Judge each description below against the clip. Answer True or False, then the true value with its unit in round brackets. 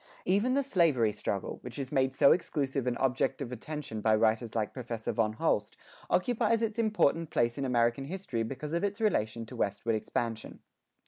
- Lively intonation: True (6.7 semitones)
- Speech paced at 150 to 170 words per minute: False (180 wpm)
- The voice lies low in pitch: True (130 Hz)